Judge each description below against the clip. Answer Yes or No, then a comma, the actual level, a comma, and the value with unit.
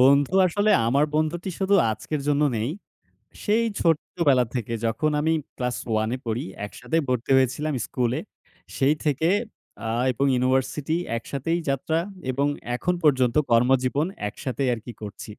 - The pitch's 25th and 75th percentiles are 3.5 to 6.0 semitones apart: Yes, average, 4.0 semitones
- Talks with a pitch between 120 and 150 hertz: Yes, low, 135 Hz